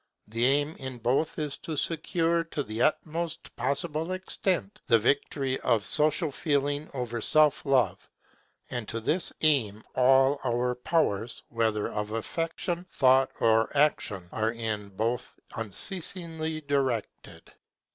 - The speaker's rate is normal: No, slow, 125 wpm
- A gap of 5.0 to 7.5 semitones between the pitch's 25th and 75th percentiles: Yes, average, 5.3 semitones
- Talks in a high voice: No, low, 135 Hz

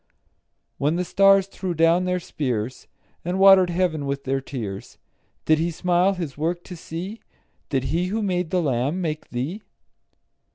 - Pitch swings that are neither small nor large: Yes, average, 4.4 semitones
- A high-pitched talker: No, medium, 170 Hz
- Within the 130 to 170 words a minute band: Yes, average, 160 wpm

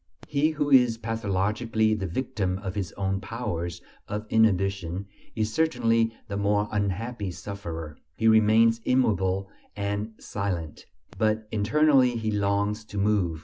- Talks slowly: Yes, slow, 130 wpm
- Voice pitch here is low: Yes, low, 105 Hz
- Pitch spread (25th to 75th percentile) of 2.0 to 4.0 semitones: Yes, average, 2.7 semitones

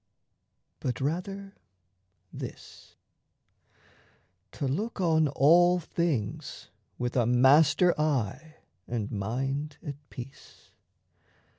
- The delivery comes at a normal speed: No, slow, 85 wpm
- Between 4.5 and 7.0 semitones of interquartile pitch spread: Yes, average, 5.2 semitones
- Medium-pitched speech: Yes, medium, 145 Hz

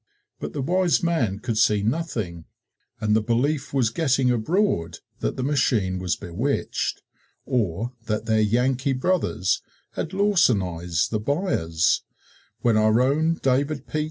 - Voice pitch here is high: No, low, 120 Hz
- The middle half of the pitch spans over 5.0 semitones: Yes, wide, 5.5 semitones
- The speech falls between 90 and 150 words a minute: Yes, slow, 135 wpm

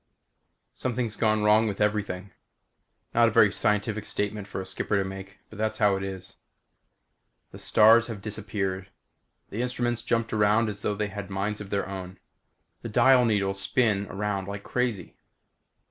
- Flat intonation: Yes, narrow, 2.3 semitones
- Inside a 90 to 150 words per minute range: No, average, 160 wpm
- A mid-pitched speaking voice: No, low, 105 Hz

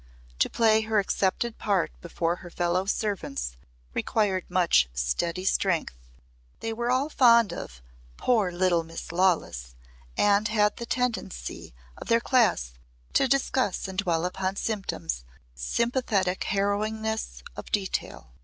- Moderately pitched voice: No, high, 195 Hz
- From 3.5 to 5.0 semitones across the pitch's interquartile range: Yes, average, 4.4 semitones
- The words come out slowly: Yes, slow, 130 wpm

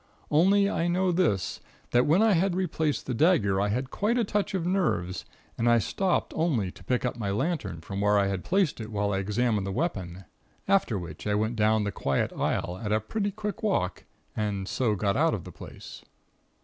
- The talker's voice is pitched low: Yes, low, 120 Hz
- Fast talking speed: Yes, fast, 210 wpm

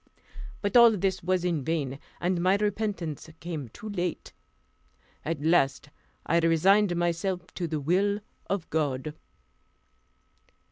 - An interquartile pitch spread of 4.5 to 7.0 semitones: No, average, 3.5 semitones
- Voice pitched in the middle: Yes, medium, 175 Hz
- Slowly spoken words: Yes, slow, 125 wpm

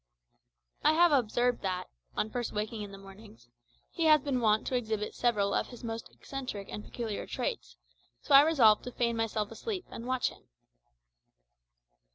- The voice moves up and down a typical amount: Yes, average, 3.6 semitones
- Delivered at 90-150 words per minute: No, average, 170 wpm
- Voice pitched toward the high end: Yes, high, 230 Hz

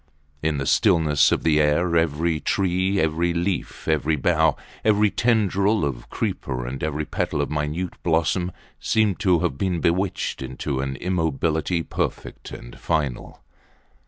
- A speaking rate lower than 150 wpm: Yes, average, 140 wpm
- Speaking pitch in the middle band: No, very low, 80 Hz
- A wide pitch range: No, average, 3.7 semitones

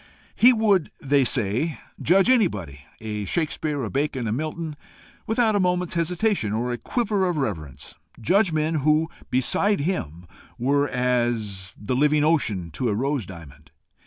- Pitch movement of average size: No, wide, 8.0 semitones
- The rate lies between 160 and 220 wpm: No, average, 150 wpm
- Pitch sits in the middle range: Yes, medium, 145 Hz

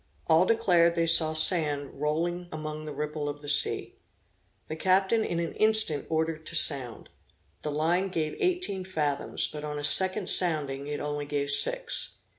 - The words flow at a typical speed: Yes, average, 165 wpm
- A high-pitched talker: No, medium, 155 Hz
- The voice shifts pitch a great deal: No, average, 3.3 semitones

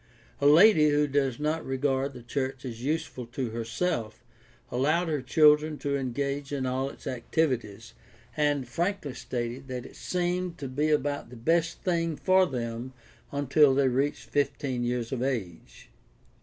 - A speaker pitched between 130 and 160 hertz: Yes, medium, 140 Hz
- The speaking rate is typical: Yes, average, 155 wpm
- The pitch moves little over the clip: No, average, 3.3 semitones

